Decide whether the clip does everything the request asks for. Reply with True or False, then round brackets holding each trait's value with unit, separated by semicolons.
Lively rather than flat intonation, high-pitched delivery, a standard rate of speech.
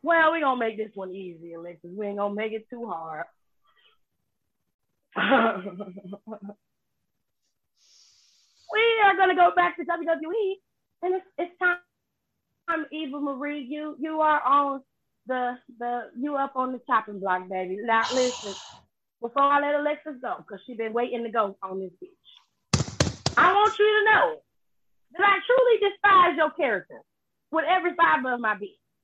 True (8.2 semitones; 280 Hz; 155 wpm)